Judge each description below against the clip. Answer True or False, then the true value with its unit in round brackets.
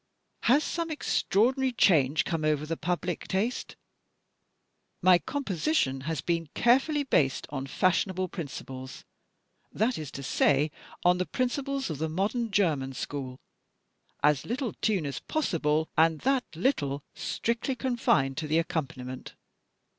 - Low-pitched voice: False (175 Hz)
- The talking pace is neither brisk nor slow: False (130 wpm)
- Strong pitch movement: True (8.5 semitones)